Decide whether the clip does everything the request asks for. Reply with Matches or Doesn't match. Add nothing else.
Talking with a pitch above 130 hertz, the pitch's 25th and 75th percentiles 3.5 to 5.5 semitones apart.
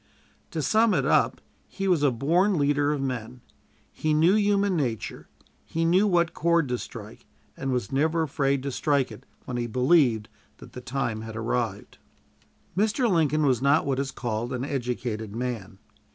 Matches